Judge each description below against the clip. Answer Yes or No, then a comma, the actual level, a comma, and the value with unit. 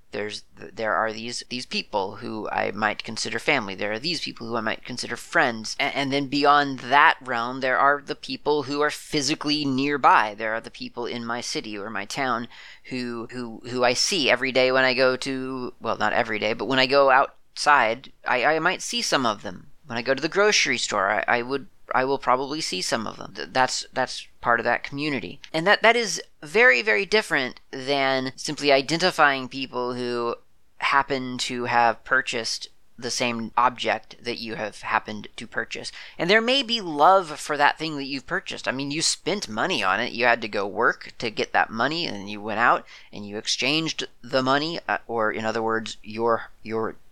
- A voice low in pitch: Yes, low, 130 Hz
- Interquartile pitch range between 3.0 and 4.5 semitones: Yes, average, 3.7 semitones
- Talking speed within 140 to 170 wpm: No, fast, 205 wpm